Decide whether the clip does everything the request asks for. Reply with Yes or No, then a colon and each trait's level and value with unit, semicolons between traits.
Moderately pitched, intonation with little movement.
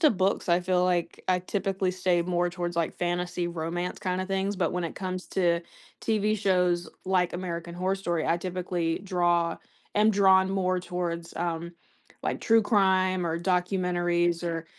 Yes: medium, 180 Hz; narrow, 1.5 semitones